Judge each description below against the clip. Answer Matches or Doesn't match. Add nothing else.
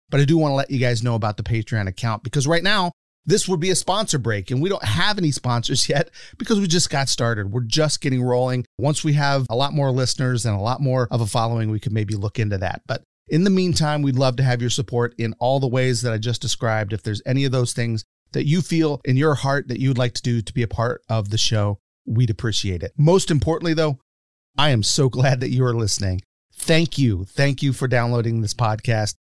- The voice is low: Matches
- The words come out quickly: Matches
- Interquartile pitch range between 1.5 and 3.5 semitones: Doesn't match